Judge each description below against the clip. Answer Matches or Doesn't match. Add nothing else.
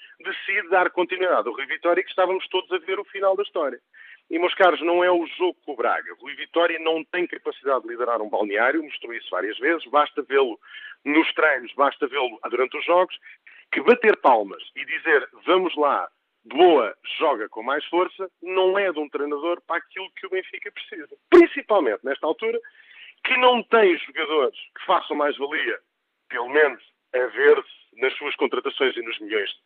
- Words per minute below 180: Doesn't match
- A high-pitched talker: Matches